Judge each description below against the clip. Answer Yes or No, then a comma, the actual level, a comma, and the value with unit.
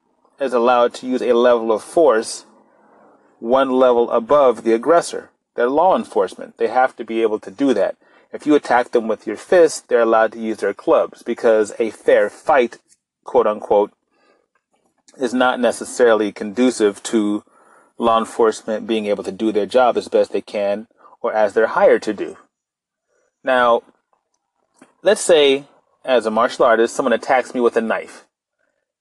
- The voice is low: Yes, low, 120 Hz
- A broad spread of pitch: No, narrow, 2.6 semitones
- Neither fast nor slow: Yes, average, 165 wpm